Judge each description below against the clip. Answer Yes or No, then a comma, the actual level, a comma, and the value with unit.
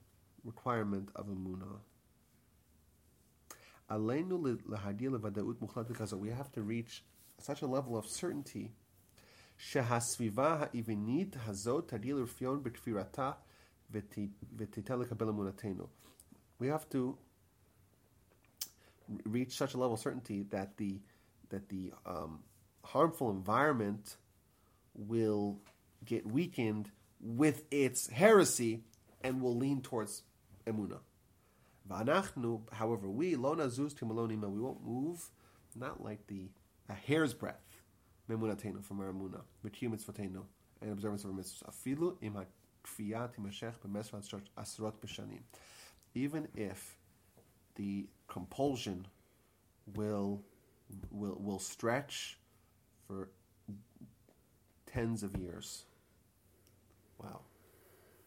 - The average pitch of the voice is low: Yes, low, 105 Hz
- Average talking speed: No, slow, 90 wpm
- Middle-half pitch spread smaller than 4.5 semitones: Yes, average, 3.1 semitones